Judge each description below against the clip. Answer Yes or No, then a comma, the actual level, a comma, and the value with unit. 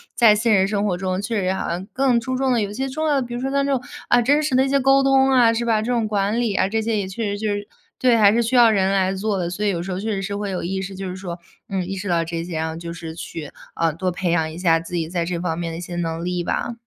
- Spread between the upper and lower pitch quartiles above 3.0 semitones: Yes, average, 4.9 semitones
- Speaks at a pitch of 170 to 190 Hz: No, high, 200 Hz